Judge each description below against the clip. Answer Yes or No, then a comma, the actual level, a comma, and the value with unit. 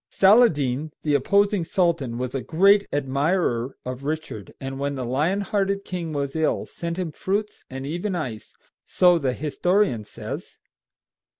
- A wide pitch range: Yes, wide, 5.8 semitones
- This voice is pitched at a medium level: Yes, medium, 155 Hz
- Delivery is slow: No, average, 145 wpm